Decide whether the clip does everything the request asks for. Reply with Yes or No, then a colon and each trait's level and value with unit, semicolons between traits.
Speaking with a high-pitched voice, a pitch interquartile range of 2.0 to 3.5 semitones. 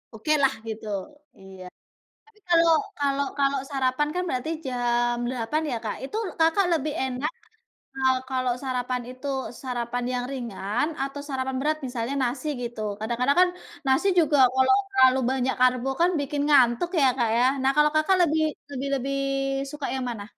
Yes: very high, 265 Hz; average, 3.1 semitones